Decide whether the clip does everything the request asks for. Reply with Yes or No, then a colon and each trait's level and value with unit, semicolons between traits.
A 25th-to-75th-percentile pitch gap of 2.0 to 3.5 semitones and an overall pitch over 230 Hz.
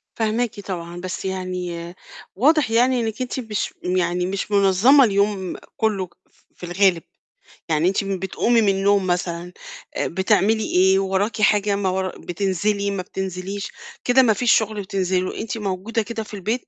No: average, 2.9 semitones; high, 195 Hz